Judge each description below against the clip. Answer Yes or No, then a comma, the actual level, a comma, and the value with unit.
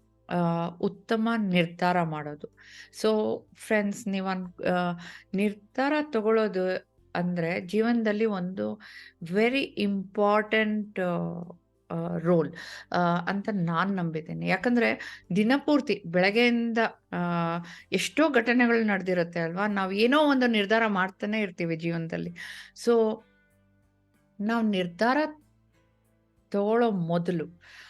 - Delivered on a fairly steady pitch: No, average, 4.5 semitones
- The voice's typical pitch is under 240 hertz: Yes, high, 190 Hz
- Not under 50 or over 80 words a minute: Yes, average, 75 wpm